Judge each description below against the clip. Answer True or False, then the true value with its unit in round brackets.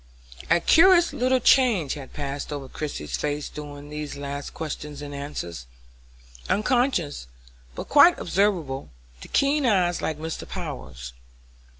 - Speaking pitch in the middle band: True (150 Hz)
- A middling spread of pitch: False (6.8 semitones)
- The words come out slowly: True (125 wpm)